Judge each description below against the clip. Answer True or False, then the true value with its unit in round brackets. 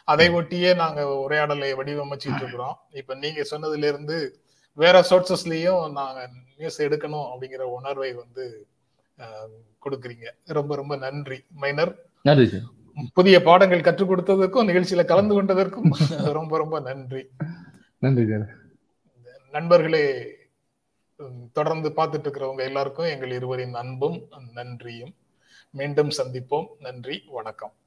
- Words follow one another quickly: False (100 wpm)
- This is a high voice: False (145 Hz)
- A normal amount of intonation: True (4.5 semitones)